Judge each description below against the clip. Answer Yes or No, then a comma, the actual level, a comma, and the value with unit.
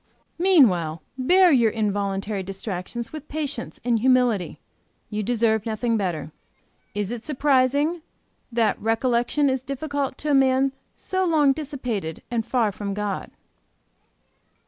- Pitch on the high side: Yes, high, 240 Hz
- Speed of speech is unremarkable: No, slow, 125 wpm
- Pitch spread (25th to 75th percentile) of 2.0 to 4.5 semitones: No, average, 5.0 semitones